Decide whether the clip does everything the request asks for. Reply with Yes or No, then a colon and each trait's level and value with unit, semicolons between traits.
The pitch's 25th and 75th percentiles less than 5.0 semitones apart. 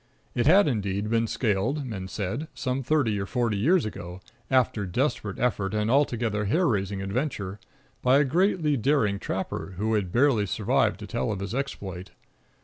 No: wide, 5.5 semitones